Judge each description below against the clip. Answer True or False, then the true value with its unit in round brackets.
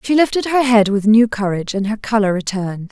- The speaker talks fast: True (225 wpm)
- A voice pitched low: False (220 Hz)